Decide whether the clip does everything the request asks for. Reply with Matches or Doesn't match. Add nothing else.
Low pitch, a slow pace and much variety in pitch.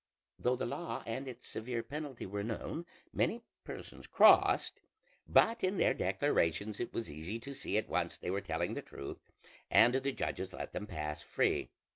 Doesn't match